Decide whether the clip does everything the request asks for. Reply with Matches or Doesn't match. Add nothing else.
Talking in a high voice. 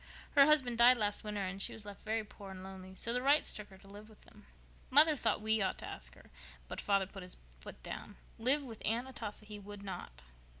Matches